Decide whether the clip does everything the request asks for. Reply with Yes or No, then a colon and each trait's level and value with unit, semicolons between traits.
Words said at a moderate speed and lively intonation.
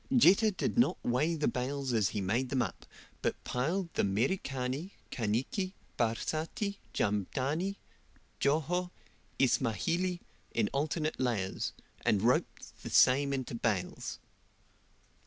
No: slow, 115 wpm; wide, 6.4 semitones